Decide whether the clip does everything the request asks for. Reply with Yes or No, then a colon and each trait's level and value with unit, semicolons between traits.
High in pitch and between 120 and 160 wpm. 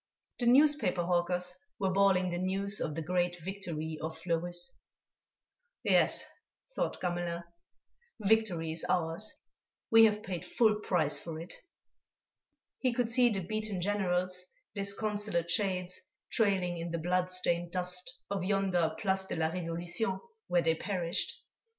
No: medium, 180 Hz; slow, 135 wpm